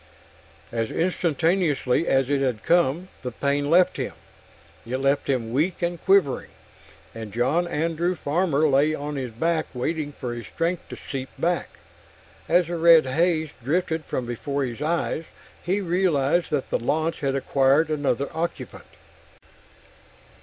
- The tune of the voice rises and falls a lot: No, average, 4.1 semitones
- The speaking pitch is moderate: Yes, medium, 150 Hz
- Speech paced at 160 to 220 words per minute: No, average, 145 wpm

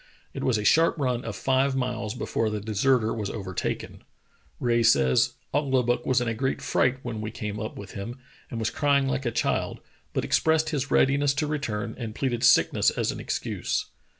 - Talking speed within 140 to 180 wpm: No, average, 195 wpm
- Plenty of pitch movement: No, average, 3.8 semitones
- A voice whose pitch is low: Yes, low, 120 Hz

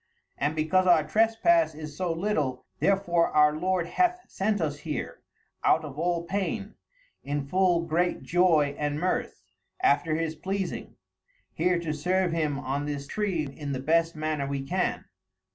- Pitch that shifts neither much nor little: Yes, average, 3.8 semitones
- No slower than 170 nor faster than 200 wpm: No, average, 155 wpm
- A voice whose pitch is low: No, medium, 165 Hz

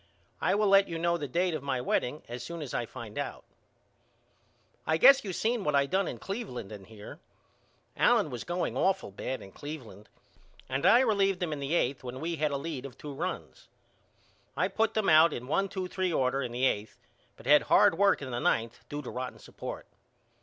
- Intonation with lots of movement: Yes, wide, 6.6 semitones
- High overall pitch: No, medium, 150 Hz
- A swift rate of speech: Yes, fast, 210 wpm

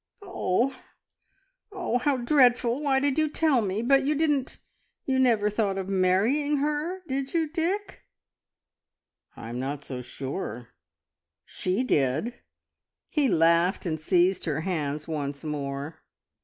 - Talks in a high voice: Yes, high, 220 Hz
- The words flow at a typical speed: No, slow, 130 wpm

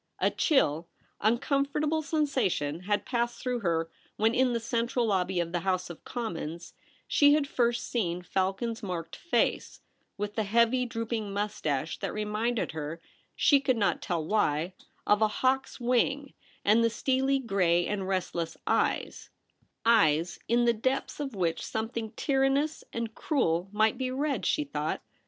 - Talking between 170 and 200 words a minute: No, average, 155 wpm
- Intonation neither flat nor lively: No, wide, 5.8 semitones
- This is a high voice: Yes, high, 225 Hz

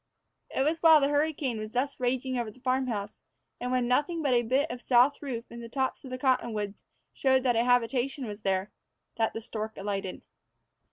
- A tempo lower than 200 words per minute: No, fast, 205 wpm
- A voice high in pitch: Yes, very high, 250 Hz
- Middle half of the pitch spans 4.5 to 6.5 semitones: No, average, 2.9 semitones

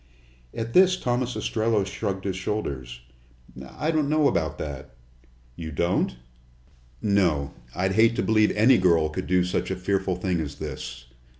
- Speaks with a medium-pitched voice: No, very low, 95 Hz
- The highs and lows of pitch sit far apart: Yes, wide, 6.1 semitones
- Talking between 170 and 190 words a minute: No, average, 155 wpm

